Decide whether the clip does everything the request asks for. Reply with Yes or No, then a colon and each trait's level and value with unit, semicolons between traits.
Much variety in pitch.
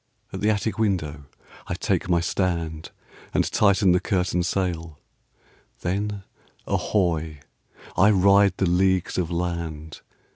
No: average, 2.9 semitones